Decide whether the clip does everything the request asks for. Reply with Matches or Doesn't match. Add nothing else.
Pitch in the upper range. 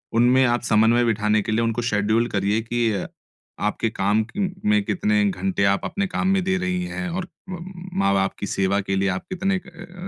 Doesn't match